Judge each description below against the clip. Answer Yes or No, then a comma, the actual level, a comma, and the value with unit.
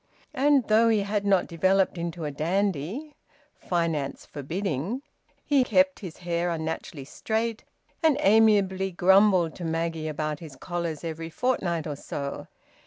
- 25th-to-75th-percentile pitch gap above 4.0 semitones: Yes, average, 4.7 semitones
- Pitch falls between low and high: Yes, medium, 175 Hz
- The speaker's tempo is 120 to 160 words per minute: Yes, slow, 135 wpm